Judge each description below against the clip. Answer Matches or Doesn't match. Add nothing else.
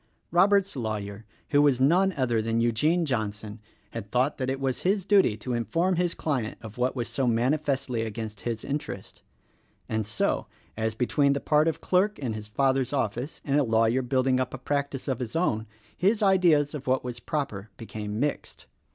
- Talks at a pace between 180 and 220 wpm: Matches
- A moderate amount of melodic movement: Matches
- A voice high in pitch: Doesn't match